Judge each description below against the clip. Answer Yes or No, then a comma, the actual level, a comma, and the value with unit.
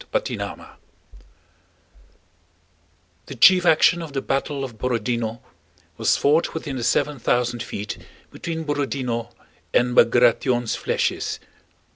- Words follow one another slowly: Yes, slow, 110 wpm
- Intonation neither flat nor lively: Yes, average, 3.8 semitones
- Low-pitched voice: Yes, low, 130 Hz